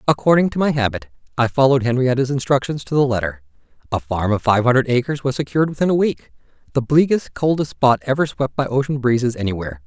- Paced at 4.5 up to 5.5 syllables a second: No, 6.5 syllables/s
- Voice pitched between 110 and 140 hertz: Yes, low, 125 Hz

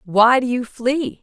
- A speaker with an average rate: Yes, average, 195 wpm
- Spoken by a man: No, female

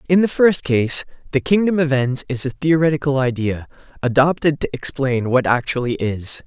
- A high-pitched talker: No, medium, 140 Hz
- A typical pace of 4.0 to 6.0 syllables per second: Yes, 5.0 syllables/s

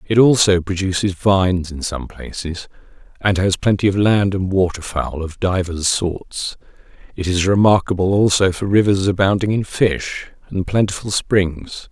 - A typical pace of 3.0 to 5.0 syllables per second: Yes, 4.5 syllables/s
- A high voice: No, very low, 95 Hz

